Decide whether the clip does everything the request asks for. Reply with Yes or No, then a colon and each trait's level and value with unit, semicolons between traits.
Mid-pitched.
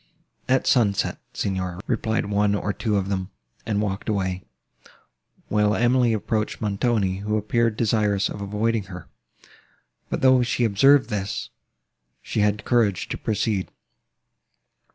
No: low, 105 Hz